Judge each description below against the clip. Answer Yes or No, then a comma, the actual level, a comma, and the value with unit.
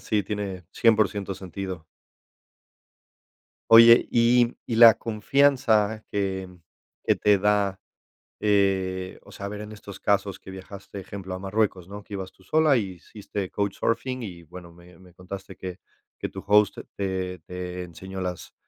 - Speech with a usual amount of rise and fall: No, narrow, 2.3 semitones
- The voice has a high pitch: No, low, 100 Hz